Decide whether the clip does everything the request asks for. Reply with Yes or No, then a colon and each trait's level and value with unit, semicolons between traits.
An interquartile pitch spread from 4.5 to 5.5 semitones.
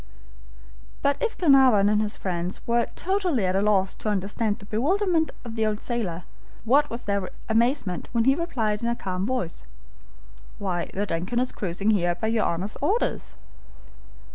Yes: average, 4.9 semitones